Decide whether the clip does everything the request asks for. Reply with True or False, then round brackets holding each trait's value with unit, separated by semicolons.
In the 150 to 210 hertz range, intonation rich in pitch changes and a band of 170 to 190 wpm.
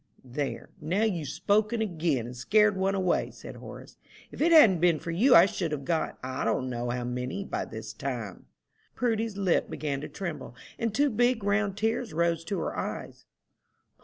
True (185 Hz; 6.3 semitones; 185 wpm)